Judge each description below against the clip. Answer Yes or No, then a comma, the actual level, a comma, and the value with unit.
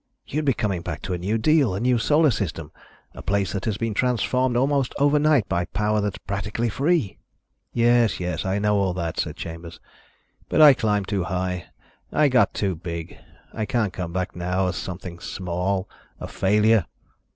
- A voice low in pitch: Yes, low, 100 Hz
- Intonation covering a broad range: No, average, 4.9 semitones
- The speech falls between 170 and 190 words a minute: Yes, average, 180 wpm